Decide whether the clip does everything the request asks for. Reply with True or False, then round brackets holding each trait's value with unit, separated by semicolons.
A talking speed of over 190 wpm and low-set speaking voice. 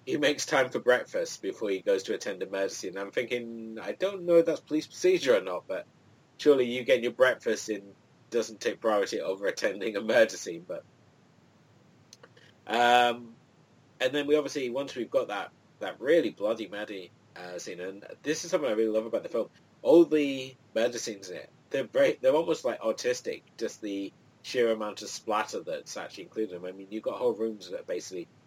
False (200 wpm; 145 Hz)